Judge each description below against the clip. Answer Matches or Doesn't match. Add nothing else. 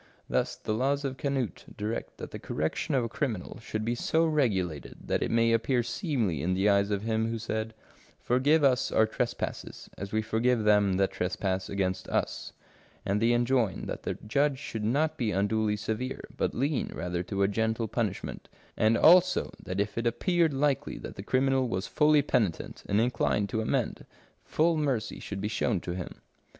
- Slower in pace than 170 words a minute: Doesn't match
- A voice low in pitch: Matches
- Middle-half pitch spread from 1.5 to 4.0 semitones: Doesn't match